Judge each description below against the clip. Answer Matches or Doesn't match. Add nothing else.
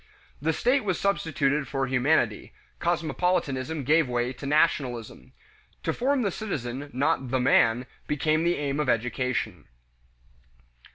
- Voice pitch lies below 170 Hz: Matches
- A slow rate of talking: Matches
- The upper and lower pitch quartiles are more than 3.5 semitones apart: Matches